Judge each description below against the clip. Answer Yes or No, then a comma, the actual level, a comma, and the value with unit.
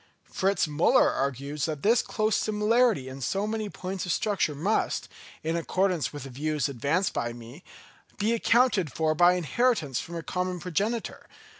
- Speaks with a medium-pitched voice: Yes, medium, 175 Hz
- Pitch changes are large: Yes, wide, 6.1 semitones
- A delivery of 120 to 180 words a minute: Yes, average, 160 wpm